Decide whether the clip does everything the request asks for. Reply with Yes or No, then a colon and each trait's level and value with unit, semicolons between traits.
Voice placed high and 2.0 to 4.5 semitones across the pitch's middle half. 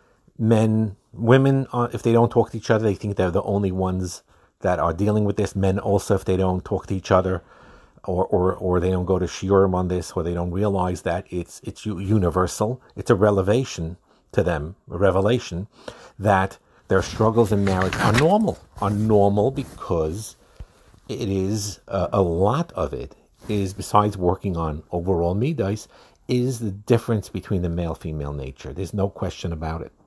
No: low, 100 Hz; average, 3.0 semitones